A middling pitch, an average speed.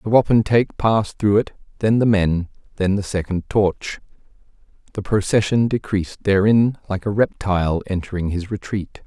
No: low, 100 Hz; average, 145 wpm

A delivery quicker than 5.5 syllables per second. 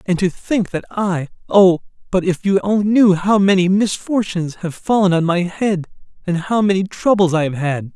No: 4.9 syllables/s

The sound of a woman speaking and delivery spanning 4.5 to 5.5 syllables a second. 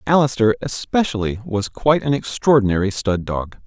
No: male; 5.3 syllables/s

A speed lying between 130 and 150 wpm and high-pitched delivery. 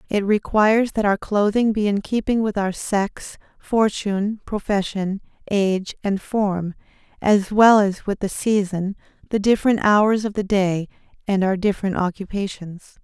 Yes: average, 145 wpm; high, 200 Hz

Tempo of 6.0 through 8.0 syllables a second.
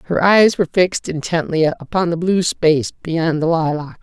No: 5.1 syllables/s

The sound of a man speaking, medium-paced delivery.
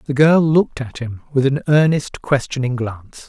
Yes: male; average, 185 wpm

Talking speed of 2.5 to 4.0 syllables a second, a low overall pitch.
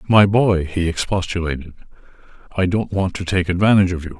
No: 6.2 syllables/s; very low, 90 Hz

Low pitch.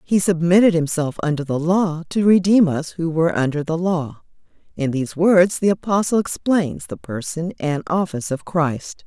No: medium, 170 Hz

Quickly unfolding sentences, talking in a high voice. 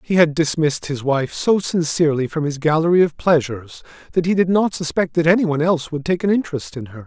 No: fast, 220 wpm; medium, 155 Hz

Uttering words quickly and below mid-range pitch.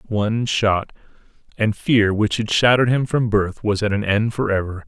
No: average, 170 wpm; low, 110 Hz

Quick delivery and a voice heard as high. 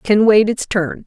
Yes: fast, 225 wpm; high, 205 Hz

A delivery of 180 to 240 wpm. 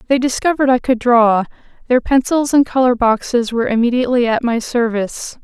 No: average, 165 wpm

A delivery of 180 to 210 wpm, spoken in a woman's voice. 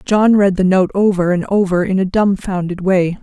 Yes: fast, 205 wpm; female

